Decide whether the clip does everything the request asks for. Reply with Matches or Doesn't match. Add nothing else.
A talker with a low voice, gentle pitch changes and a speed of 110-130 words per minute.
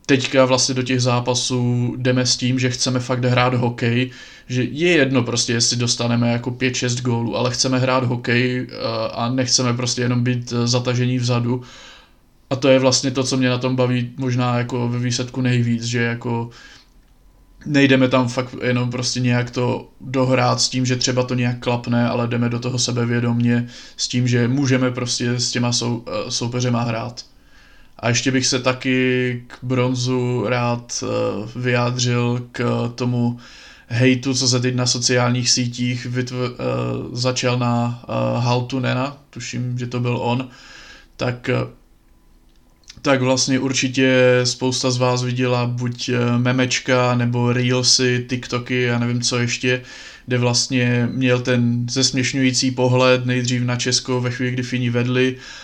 Doesn't match